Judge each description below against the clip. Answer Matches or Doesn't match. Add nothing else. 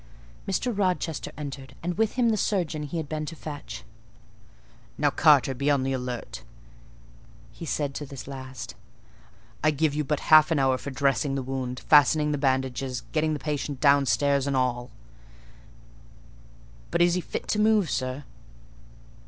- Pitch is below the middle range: Doesn't match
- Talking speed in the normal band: Matches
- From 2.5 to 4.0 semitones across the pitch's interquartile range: Matches